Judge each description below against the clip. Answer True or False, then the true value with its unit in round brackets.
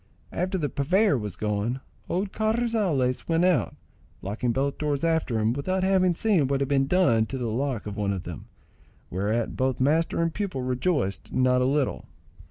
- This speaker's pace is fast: False (180 wpm)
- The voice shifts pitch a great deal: True (7.1 semitones)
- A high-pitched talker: False (135 Hz)